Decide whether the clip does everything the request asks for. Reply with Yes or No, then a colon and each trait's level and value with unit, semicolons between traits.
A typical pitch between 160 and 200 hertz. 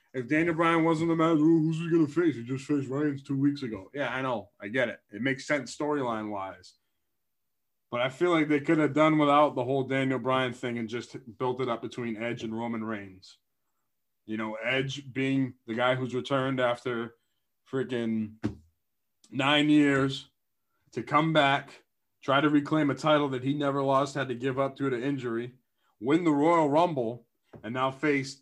No: low, 135 Hz